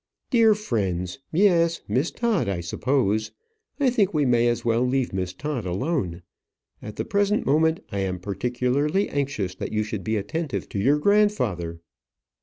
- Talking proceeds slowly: No, average, 160 wpm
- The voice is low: Yes, low, 125 Hz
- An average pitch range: No, wide, 9.0 semitones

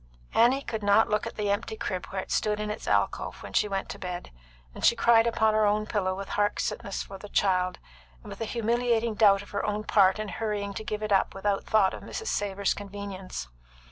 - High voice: Yes, high, 205 Hz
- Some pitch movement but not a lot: No, narrow, 1.7 semitones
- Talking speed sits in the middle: No, fast, 230 wpm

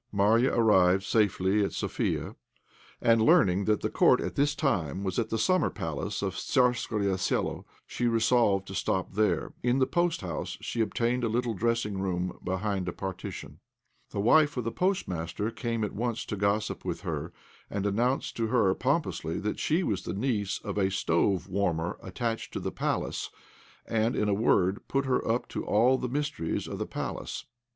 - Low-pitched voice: Yes, low, 105 Hz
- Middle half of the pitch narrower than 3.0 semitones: No, average, 4.1 semitones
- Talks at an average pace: Yes, average, 180 wpm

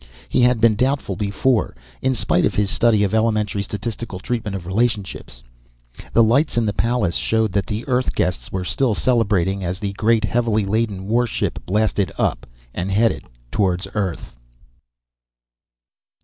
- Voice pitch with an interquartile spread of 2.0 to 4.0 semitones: Yes, average, 3.1 semitones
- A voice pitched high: No, low, 105 Hz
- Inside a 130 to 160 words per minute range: Yes, average, 150 wpm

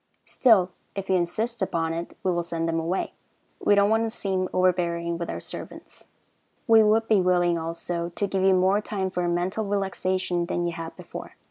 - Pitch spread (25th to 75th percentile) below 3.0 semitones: Yes, narrow, 2.6 semitones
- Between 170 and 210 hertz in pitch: Yes, medium, 185 Hz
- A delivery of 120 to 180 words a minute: No, average, 195 wpm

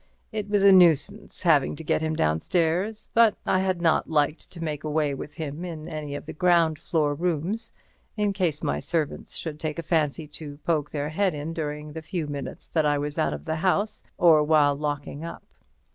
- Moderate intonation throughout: Yes, average, 3.0 semitones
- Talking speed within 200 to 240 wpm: Yes, fast, 205 wpm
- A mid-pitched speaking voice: Yes, medium, 155 Hz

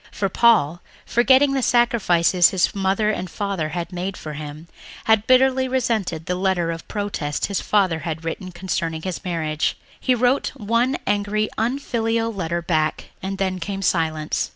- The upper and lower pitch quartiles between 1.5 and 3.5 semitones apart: No, average, 5.2 semitones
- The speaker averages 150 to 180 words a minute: Yes, average, 155 wpm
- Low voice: No, high, 190 Hz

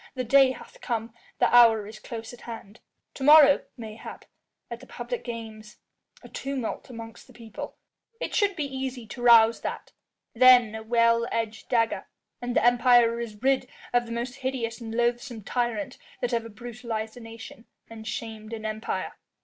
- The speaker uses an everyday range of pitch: No, narrow, 1.8 semitones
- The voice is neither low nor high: No, high, 235 Hz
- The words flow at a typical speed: Yes, average, 170 wpm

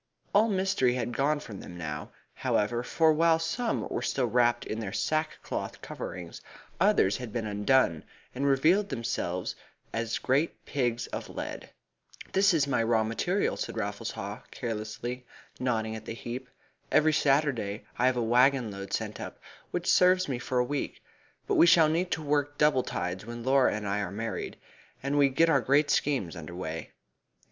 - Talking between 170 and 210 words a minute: Yes, average, 175 wpm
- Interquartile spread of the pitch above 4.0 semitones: Yes, average, 5.1 semitones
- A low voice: Yes, low, 125 Hz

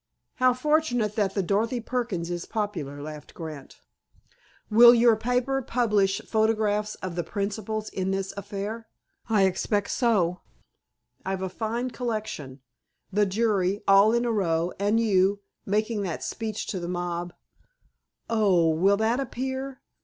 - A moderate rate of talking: No, slow, 130 wpm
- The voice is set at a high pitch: Yes, high, 205 Hz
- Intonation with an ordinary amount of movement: Yes, average, 3.6 semitones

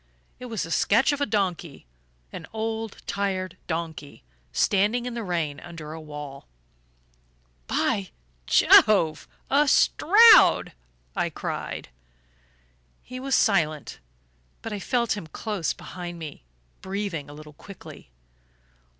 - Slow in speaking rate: Yes, slow, 120 wpm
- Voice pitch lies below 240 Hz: Yes, high, 190 Hz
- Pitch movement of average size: No, wide, 6.2 semitones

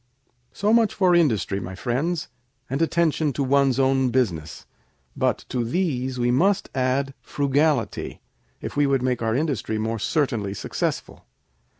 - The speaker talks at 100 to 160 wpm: Yes, average, 140 wpm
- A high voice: No, low, 135 Hz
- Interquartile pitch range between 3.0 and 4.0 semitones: No, average, 4.4 semitones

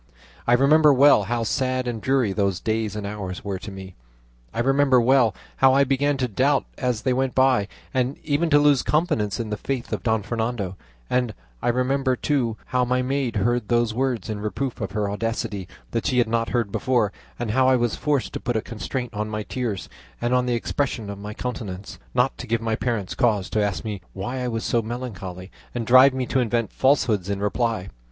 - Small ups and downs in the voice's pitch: No, average, 3.5 semitones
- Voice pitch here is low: Yes, low, 120 Hz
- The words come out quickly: Yes, fast, 210 wpm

